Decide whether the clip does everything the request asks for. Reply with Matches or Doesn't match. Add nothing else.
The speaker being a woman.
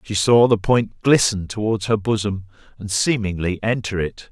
Doesn't match